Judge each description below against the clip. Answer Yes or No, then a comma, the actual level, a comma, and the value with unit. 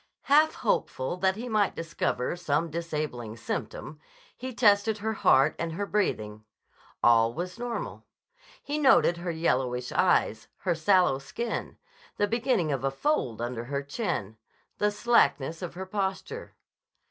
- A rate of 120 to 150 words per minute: Yes, average, 140 wpm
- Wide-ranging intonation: Yes, wide, 7.8 semitones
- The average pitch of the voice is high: No, medium, 170 Hz